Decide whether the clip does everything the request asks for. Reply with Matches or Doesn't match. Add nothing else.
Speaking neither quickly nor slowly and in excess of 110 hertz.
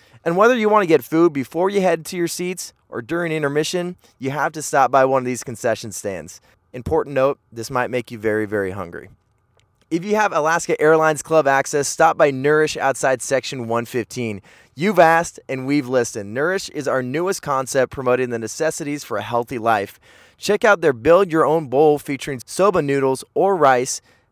Matches